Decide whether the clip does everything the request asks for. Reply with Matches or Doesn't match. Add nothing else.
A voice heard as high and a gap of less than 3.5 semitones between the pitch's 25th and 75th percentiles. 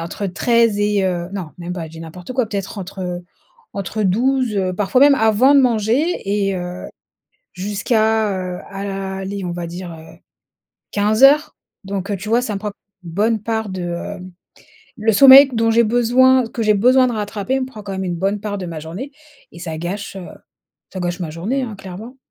Doesn't match